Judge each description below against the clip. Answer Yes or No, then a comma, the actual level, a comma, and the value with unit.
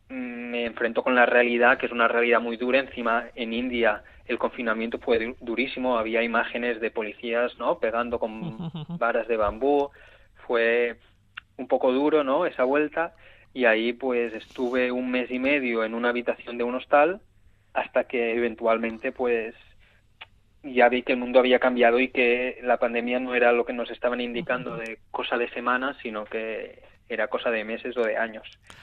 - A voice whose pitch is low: Yes, low, 120 Hz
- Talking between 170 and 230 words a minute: Yes, average, 175 wpm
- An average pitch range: No, narrow, 1.6 semitones